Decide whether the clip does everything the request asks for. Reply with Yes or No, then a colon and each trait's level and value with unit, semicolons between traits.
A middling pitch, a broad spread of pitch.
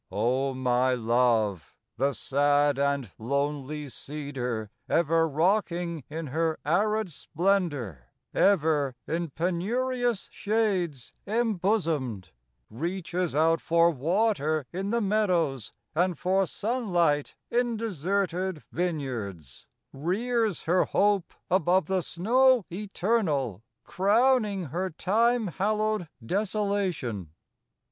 Yes: medium, 170 Hz; wide, 6.3 semitones